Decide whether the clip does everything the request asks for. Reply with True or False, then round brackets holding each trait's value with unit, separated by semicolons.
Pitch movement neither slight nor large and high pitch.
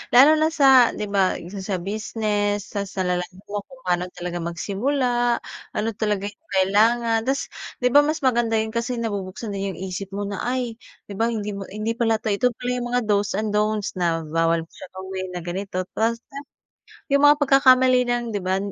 True (4.0 semitones; 210 Hz)